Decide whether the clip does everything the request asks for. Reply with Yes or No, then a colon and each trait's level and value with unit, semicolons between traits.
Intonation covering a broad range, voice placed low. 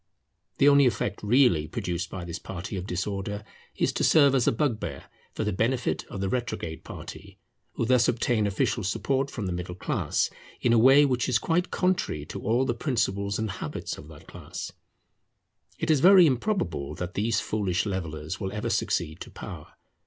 Yes: wide, 5.9 semitones; low, 105 Hz